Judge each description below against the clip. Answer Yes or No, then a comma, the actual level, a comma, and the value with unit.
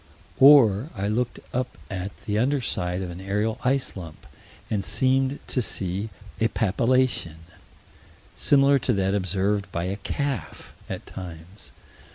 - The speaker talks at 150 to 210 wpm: No, average, 140 wpm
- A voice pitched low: Yes, low, 105 Hz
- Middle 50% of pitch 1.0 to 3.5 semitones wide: No, wide, 5.4 semitones